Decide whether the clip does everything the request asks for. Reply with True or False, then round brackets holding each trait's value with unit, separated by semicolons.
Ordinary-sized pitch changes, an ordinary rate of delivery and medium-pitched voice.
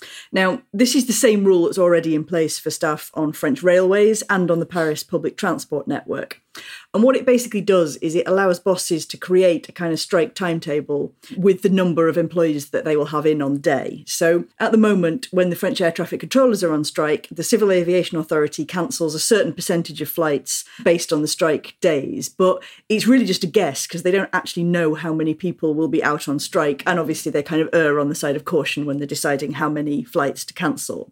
False (3.4 semitones; 225 wpm; 170 Hz)